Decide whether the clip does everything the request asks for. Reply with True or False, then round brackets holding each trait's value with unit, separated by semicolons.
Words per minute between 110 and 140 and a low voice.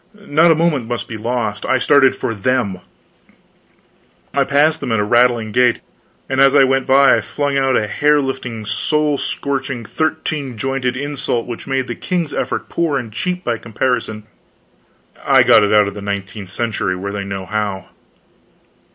False (175 wpm; 125 Hz)